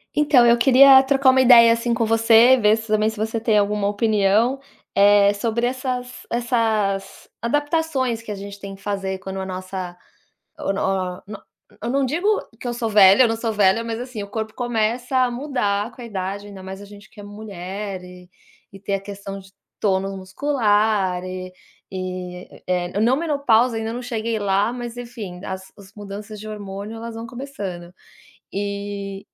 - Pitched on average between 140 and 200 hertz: No, high, 215 Hz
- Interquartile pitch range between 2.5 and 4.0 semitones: Yes, average, 3.4 semitones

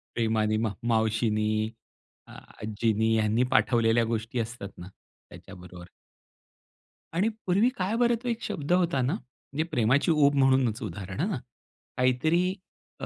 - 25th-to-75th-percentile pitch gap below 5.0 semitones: No, wide, 5.4 semitones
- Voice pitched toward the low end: Yes, low, 120 Hz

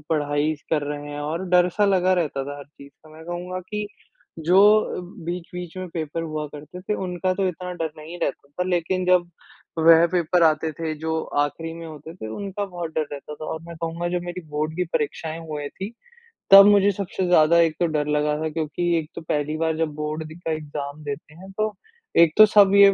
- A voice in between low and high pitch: Yes, medium, 165 Hz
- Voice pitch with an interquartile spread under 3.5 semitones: Yes, average, 2.9 semitones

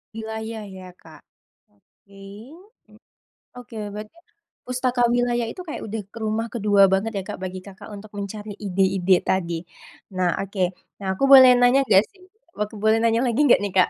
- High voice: Yes, high, 215 Hz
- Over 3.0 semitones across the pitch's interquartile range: Yes, average, 3.4 semitones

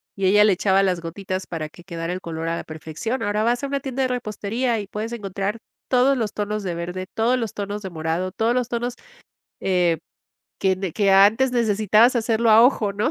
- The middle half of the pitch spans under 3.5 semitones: No, average, 3.9 semitones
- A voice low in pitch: No, high, 205 Hz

